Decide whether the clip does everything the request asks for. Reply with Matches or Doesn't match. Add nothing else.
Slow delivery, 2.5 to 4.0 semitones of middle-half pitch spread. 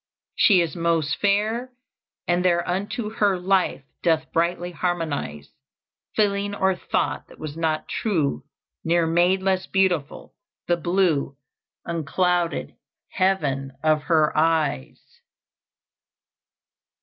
Matches